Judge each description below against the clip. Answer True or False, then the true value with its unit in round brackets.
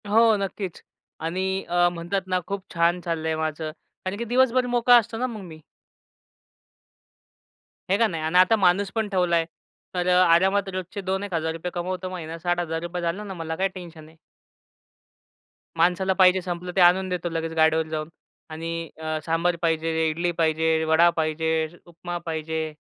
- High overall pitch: False (175 Hz)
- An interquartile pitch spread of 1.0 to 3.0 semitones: True (2.7 semitones)